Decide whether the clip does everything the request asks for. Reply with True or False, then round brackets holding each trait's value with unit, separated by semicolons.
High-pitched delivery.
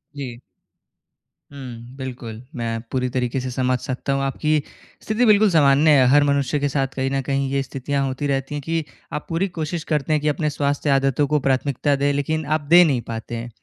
False (140 Hz)